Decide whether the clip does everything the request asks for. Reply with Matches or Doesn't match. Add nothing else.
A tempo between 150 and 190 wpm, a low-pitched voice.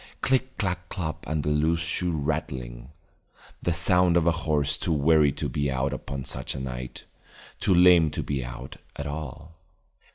Matches